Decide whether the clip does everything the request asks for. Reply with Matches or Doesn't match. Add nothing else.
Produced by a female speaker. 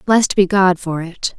Matches